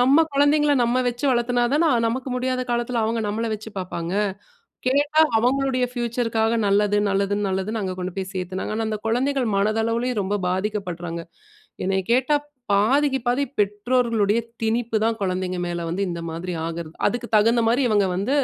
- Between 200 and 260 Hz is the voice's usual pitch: Yes, high, 225 Hz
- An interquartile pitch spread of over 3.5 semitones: Yes, average, 4.2 semitones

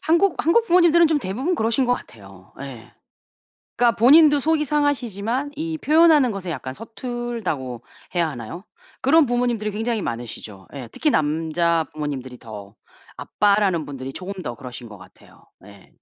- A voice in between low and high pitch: No, high, 205 Hz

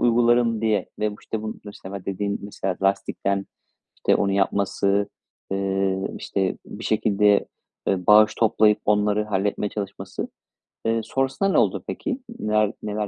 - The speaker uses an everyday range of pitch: No, narrow, 1.7 semitones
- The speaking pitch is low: Yes, low, 105 Hz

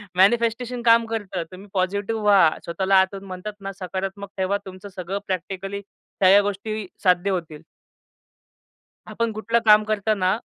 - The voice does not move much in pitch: Yes, narrow, 2.3 semitones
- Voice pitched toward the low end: No, high, 200 Hz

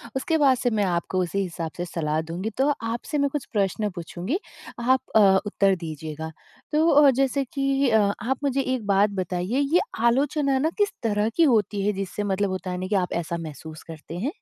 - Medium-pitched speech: No, high, 205 Hz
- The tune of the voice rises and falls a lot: Yes, wide, 7.2 semitones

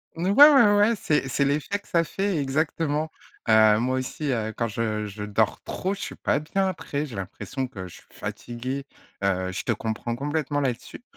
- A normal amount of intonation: No, wide, 6.5 semitones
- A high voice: No, low, 135 Hz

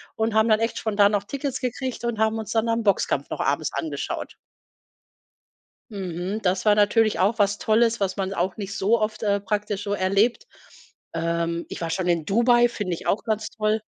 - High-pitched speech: Yes, high, 210 Hz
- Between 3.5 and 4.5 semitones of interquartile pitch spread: No, narrow, 2.6 semitones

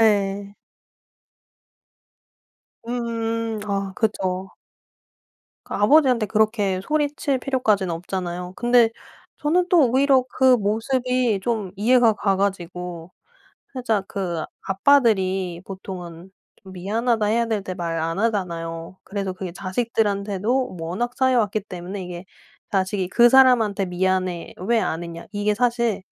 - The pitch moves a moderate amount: Yes, average, 4.3 semitones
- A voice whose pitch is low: No, high, 205 Hz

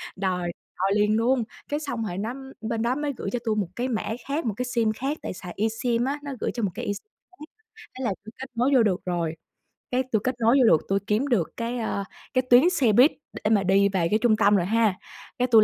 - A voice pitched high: Yes, high, 225 Hz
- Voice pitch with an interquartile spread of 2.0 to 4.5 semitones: Yes, average, 3.9 semitones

